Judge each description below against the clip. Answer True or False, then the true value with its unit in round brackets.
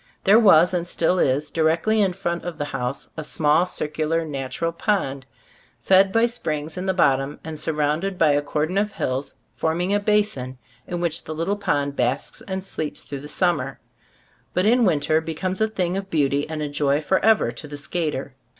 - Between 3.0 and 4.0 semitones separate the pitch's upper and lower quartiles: False (4.4 semitones)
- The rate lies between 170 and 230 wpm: True (185 wpm)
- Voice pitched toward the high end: False (160 Hz)